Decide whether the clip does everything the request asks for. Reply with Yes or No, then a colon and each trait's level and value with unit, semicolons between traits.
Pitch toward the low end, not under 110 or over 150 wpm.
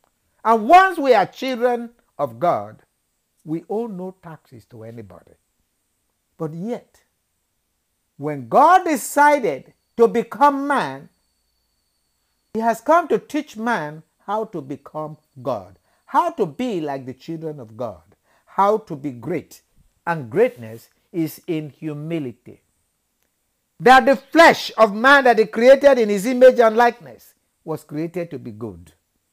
No: medium, 165 Hz; slow, 135 wpm